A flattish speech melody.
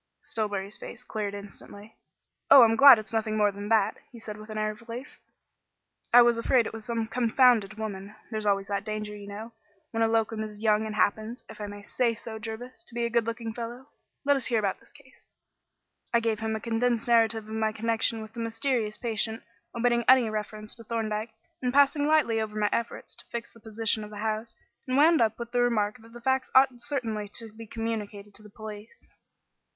Yes: narrow, 1.9 semitones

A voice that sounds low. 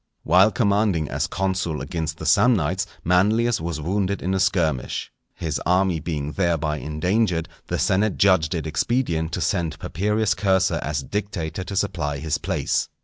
Yes: very low, 90 Hz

